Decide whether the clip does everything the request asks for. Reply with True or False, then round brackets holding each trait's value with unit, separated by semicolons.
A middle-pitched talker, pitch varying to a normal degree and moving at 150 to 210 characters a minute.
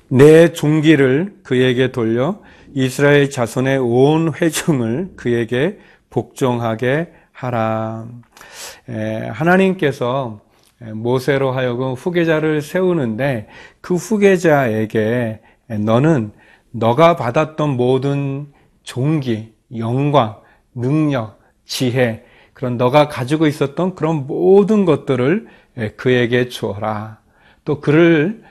False (130 Hz; 4.7 semitones; 205 characters per minute)